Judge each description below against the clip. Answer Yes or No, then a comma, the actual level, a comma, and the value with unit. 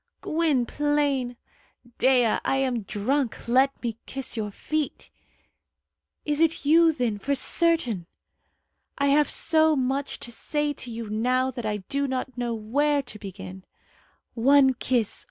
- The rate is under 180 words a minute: Yes, slow, 135 wpm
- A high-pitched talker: Yes, very high, 260 Hz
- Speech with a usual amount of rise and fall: Yes, average, 3.9 semitones